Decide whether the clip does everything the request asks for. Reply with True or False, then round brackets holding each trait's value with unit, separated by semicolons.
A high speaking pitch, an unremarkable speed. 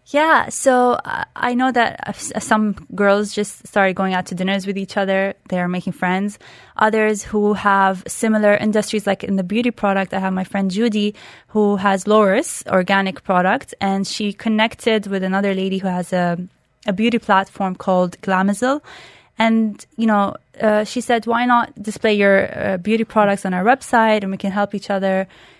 True (205 Hz; 180 wpm)